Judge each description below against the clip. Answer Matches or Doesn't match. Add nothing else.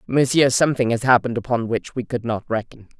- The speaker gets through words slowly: Doesn't match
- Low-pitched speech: Matches